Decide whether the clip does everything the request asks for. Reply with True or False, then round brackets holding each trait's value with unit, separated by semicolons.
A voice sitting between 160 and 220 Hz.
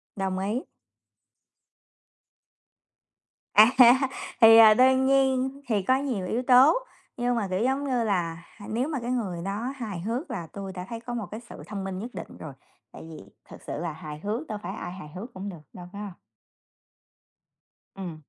True (215 Hz)